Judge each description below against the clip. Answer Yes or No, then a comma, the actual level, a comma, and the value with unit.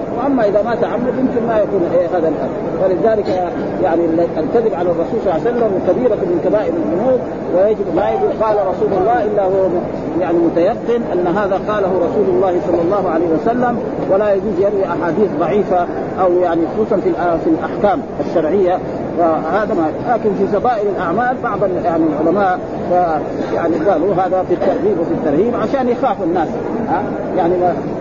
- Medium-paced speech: No, fast, 160 wpm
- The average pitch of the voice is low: No, high, 190 Hz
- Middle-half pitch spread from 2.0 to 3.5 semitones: No, average, 4.2 semitones